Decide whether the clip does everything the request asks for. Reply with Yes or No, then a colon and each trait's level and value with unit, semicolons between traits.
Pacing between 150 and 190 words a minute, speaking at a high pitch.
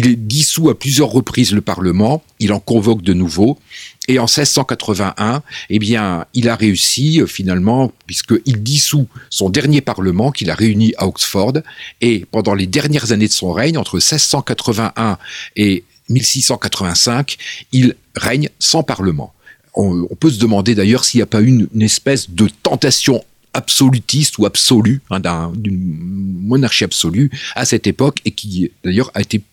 No: average, 160 wpm; low, 115 Hz